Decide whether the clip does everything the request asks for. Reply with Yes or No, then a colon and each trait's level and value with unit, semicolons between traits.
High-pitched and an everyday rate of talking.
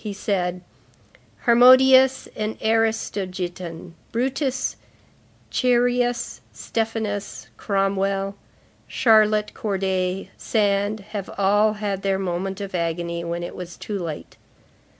No: high, 200 Hz; slow, 95 wpm